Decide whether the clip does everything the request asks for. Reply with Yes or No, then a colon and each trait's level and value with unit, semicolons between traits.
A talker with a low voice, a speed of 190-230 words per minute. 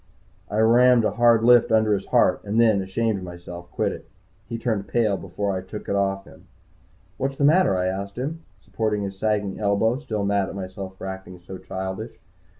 Yes: low, 100 Hz; average, 200 wpm